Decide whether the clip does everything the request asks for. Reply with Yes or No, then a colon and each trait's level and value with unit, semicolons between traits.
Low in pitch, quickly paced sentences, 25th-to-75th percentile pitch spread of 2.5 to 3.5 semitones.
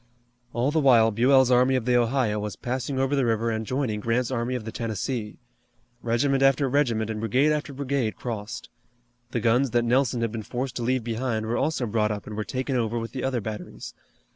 Yes: low, 120 Hz; fast, 210 wpm; average, 2.8 semitones